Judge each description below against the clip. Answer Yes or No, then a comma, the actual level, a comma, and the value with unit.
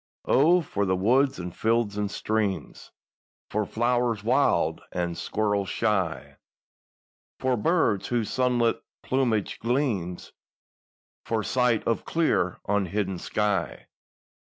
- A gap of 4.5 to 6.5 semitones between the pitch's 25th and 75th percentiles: No, average, 4.0 semitones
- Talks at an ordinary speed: No, slow, 105 wpm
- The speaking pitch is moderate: No, low, 110 Hz